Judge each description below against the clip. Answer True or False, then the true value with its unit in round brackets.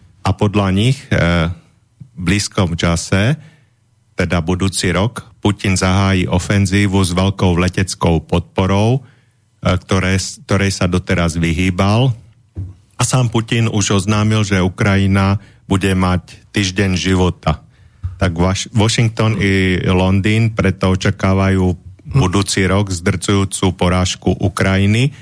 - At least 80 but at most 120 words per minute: True (110 wpm)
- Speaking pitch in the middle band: False (95 Hz)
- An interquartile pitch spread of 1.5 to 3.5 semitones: True (2.5 semitones)